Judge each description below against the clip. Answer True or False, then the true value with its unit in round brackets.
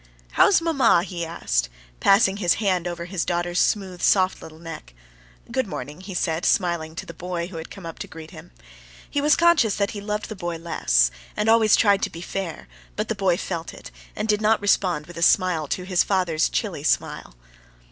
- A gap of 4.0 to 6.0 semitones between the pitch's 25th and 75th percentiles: False (3.4 semitones)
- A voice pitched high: False (180 Hz)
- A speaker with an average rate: False (210 wpm)